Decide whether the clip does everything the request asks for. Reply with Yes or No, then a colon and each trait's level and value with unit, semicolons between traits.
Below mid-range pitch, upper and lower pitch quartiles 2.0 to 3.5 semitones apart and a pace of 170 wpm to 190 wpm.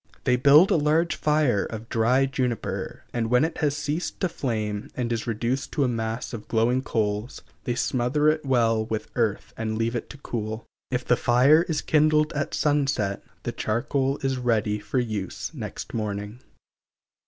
No: low, 125 Hz; average, 4.1 semitones; average, 175 wpm